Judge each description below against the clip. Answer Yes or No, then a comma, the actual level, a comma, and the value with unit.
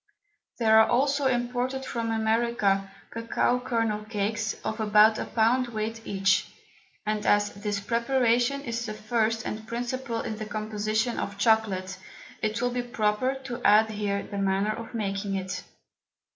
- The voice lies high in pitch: Yes, high, 220 Hz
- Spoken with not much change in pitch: Yes, narrow, 2.3 semitones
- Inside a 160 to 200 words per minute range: No, average, 150 wpm